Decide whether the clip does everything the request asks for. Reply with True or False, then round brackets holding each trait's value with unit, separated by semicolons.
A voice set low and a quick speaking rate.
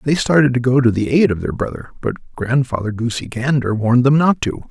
True (125 Hz; 230 wpm)